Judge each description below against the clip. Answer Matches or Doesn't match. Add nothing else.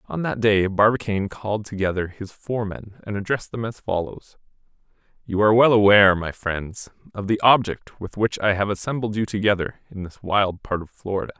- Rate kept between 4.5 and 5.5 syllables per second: Doesn't match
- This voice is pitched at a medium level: Doesn't match